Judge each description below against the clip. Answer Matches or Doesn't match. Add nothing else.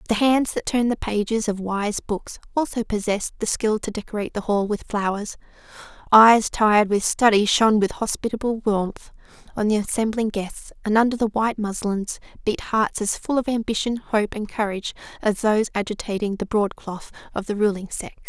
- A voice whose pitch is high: Matches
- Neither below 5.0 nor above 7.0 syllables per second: Matches